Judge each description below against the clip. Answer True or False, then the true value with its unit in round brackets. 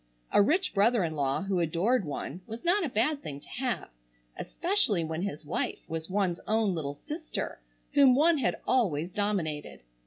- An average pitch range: False (8.1 semitones)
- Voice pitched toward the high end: True (200 Hz)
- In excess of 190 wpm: False (175 wpm)